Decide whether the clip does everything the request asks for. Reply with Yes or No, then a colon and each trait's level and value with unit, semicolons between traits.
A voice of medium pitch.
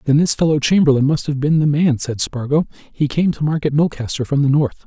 Yes: medium, 145 Hz